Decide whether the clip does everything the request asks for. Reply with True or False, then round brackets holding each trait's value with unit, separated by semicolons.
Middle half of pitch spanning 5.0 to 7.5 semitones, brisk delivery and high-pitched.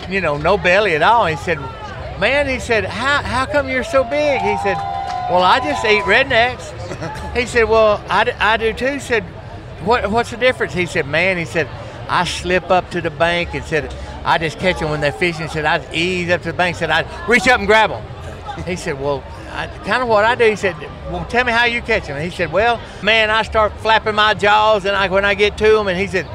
True (5.3 semitones; 250 wpm; 200 Hz)